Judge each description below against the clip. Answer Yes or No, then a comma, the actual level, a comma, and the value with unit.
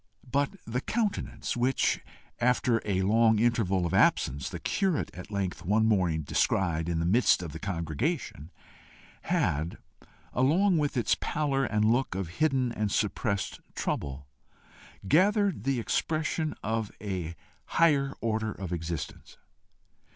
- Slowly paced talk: Yes, slow, 130 wpm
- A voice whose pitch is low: Yes, low, 110 Hz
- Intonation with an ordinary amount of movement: No, wide, 7.0 semitones